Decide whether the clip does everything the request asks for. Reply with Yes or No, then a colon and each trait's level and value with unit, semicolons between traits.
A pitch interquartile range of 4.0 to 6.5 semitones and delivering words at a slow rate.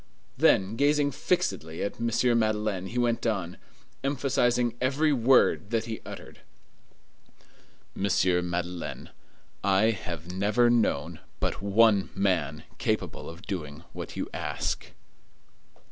Yes: average, 5.0 semitones; slow, 115 wpm